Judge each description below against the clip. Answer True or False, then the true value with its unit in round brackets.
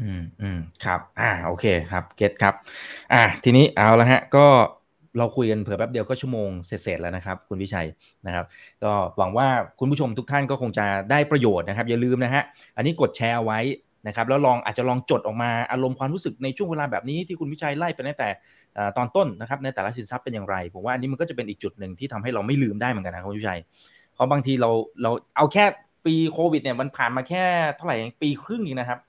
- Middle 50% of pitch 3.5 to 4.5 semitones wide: False (5.0 semitones)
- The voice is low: True (125 Hz)